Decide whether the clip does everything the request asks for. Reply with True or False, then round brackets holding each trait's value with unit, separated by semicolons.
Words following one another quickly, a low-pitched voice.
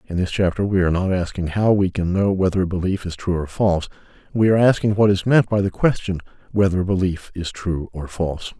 True (235 wpm; 95 Hz)